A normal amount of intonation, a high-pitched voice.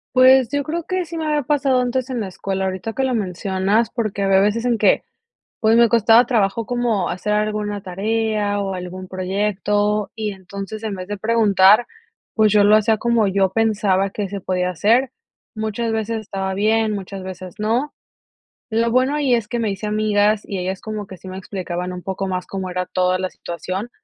Yes: average, 3.1 semitones; high, 210 Hz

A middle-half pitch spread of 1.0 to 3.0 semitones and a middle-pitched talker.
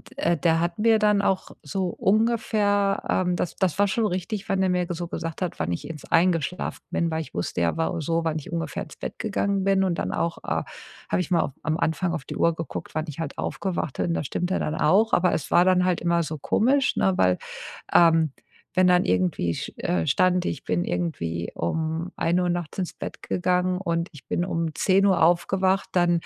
Yes: average, 2.7 semitones; medium, 175 Hz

